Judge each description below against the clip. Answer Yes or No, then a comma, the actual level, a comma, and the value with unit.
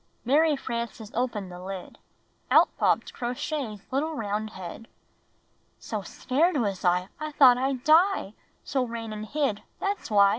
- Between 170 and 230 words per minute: No, average, 155 wpm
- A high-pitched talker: Yes, high, 240 Hz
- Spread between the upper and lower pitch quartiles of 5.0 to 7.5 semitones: Yes, wide, 5.6 semitones